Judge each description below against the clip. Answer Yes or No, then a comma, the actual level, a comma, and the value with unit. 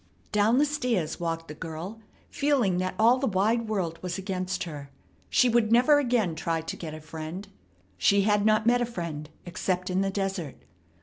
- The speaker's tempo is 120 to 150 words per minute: No, average, 185 wpm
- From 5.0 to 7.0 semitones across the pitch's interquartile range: Yes, wide, 5.4 semitones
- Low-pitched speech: No, high, 195 Hz